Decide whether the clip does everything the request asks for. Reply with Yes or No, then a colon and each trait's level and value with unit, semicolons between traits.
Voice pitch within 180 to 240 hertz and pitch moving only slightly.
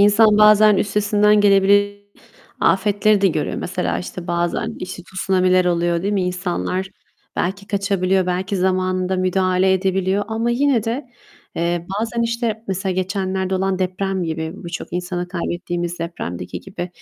Yes: high, 190 Hz; narrow, 2.2 semitones